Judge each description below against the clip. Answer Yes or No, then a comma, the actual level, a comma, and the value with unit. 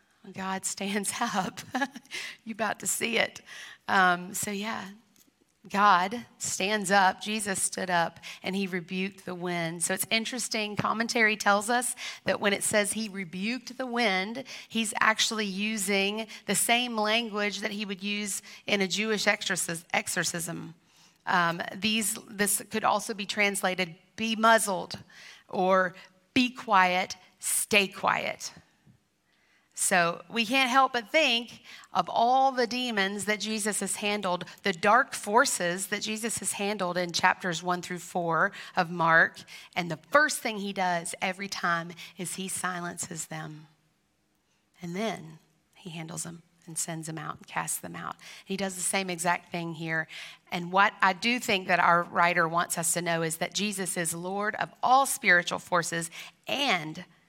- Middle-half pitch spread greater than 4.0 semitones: No, average, 3.5 semitones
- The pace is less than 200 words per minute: Yes, average, 155 wpm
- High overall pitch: Yes, high, 195 Hz